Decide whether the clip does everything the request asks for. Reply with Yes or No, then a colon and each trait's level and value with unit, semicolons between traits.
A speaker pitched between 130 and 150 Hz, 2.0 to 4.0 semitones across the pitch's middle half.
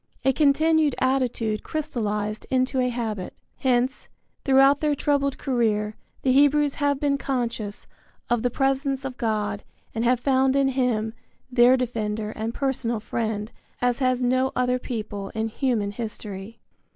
No: very high, 250 Hz; average, 3.5 semitones